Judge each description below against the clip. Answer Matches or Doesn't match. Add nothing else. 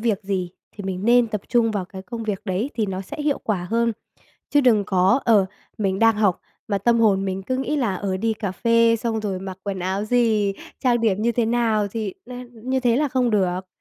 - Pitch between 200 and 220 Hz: Matches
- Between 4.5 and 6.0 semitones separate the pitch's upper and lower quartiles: Doesn't match